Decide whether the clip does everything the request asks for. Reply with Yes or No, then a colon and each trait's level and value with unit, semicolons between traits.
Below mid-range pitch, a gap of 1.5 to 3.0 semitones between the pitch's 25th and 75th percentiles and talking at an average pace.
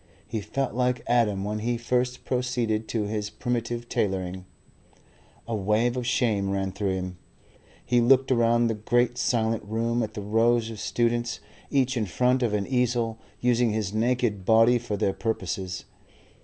Yes: low, 115 Hz; average, 2.7 semitones; average, 160 wpm